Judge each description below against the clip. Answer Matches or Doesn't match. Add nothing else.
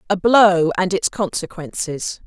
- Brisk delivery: Doesn't match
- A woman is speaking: Matches